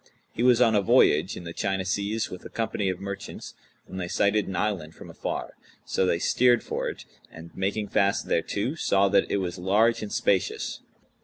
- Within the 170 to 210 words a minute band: Yes, average, 200 wpm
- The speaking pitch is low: Yes, low, 100 Hz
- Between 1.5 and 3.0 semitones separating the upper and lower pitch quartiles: Yes, narrow, 2.5 semitones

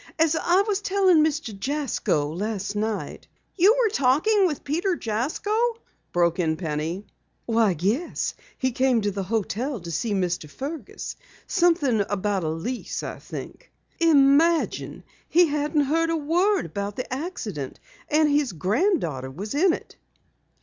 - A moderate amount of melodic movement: No, wide, 8.8 semitones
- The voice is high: Yes, very high, 265 Hz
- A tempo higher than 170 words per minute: No, average, 145 wpm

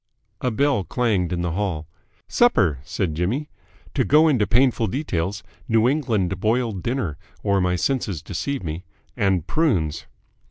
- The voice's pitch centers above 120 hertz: No, low, 105 Hz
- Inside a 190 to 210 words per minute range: No, average, 145 wpm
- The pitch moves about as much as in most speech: No, wide, 6.5 semitones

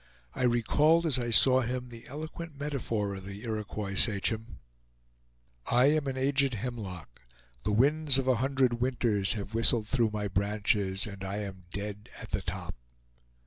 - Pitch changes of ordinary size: Yes, average, 4.3 semitones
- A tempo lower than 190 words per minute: Yes, average, 160 wpm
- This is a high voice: No, low, 115 Hz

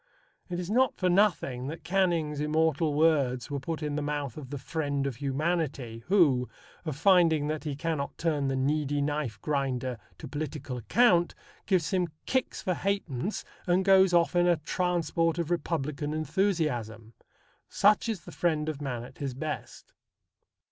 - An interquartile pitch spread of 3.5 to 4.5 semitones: Yes, average, 4.0 semitones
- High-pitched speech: No, medium, 155 Hz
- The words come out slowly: No, average, 160 wpm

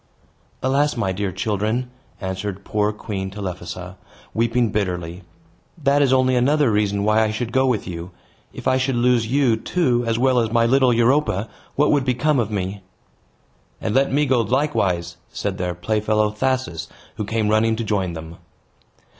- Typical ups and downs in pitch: Yes, average, 4.6 semitones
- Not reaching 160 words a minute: No, average, 165 wpm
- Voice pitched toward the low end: Yes, low, 110 Hz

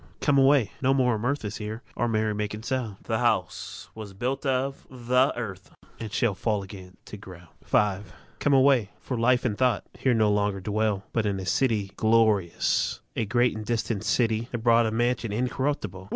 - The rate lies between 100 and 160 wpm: No, average, 185 wpm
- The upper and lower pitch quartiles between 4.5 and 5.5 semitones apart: No, average, 3.3 semitones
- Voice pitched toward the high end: No, low, 110 Hz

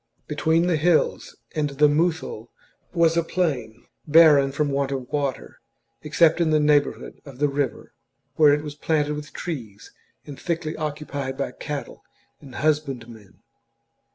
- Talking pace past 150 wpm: No, average, 145 wpm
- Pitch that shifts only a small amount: Yes, narrow, 2.3 semitones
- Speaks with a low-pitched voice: No, medium, 150 Hz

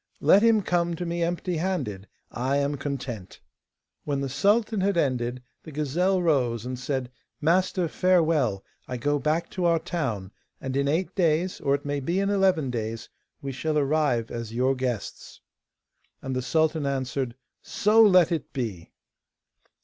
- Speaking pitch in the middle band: Yes, medium, 145 Hz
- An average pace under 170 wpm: Yes, average, 160 wpm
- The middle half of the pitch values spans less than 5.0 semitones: No, average, 5.3 semitones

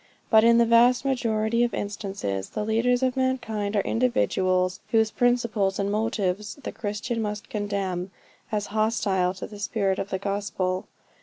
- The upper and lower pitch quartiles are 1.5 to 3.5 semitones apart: Yes, average, 2.9 semitones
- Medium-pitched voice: No, high, 210 Hz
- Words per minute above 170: No, average, 155 wpm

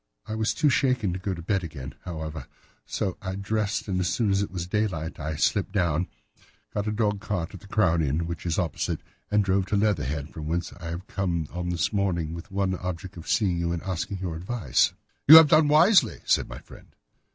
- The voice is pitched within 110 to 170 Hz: No, very low, 95 Hz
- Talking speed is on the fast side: Yes, fast, 220 wpm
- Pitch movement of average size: Yes, average, 3.6 semitones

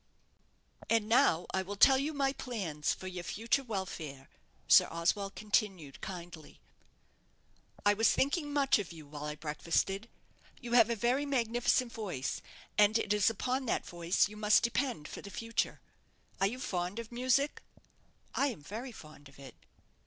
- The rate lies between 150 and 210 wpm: Yes, average, 160 wpm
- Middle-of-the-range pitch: No, high, 210 Hz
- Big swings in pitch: Yes, wide, 5.8 semitones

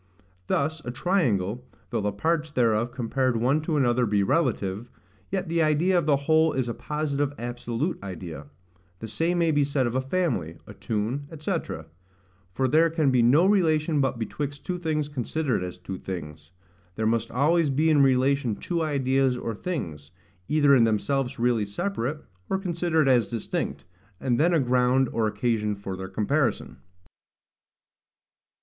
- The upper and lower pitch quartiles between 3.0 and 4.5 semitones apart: No, wide, 5.4 semitones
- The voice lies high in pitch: No, low, 135 Hz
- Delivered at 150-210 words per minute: Yes, average, 160 wpm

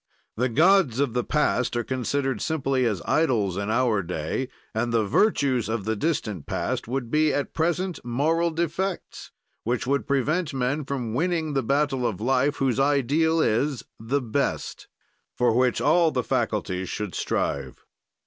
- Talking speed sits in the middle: Yes, average, 160 wpm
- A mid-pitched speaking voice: No, low, 130 Hz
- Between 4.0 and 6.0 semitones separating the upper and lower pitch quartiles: Yes, average, 4.7 semitones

